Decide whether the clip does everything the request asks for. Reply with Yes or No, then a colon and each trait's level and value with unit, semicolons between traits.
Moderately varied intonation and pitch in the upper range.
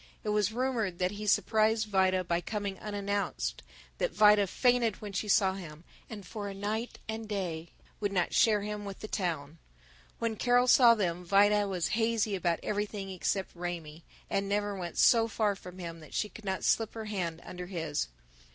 Yes: average, 3.0 semitones; high, 200 Hz